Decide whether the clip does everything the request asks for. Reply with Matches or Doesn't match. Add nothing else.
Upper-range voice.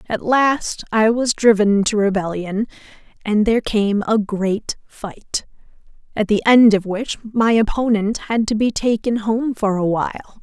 Matches